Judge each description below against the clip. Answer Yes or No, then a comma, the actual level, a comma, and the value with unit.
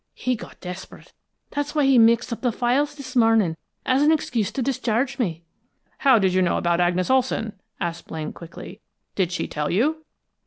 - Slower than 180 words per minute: No, average, 185 wpm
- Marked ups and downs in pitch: Yes, wide, 6.6 semitones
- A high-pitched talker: Yes, high, 230 Hz